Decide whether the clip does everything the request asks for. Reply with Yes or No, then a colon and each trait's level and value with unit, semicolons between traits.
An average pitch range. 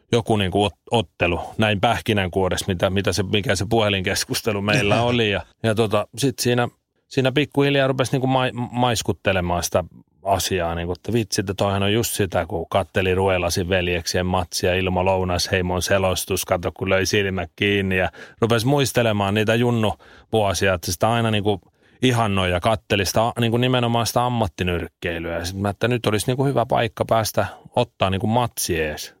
Yes: average, 3.9 semitones